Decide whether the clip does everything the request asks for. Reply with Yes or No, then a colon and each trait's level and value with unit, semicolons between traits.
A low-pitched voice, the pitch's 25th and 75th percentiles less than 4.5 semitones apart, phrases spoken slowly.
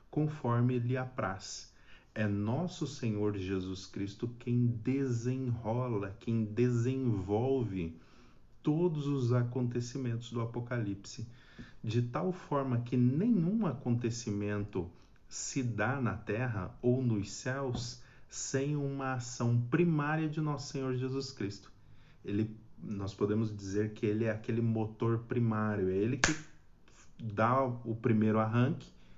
Yes: low, 120 Hz; average, 3.4 semitones; slow, 115 wpm